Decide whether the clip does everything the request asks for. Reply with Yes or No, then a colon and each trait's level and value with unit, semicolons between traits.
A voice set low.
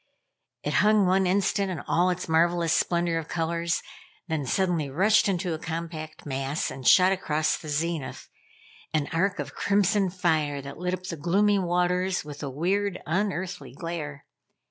No: medium, 170 Hz